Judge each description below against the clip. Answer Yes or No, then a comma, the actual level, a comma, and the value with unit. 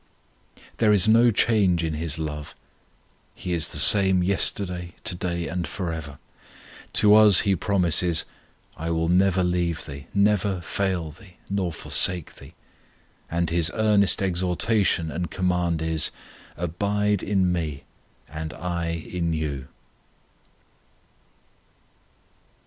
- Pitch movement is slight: No, average, 3.1 semitones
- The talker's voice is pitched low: Yes, very low, 90 Hz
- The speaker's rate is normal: No, slow, 120 wpm